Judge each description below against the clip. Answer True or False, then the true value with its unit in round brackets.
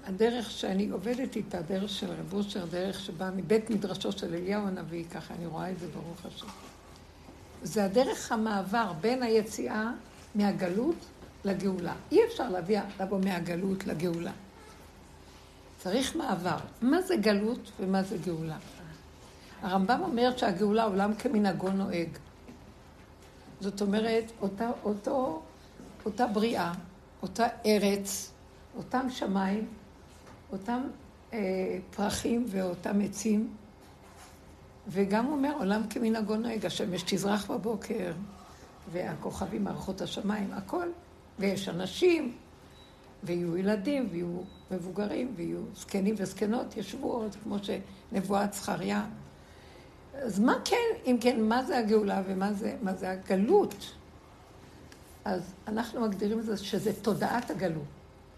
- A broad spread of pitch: False (3.5 semitones)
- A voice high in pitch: True (205 Hz)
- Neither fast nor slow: True (110 wpm)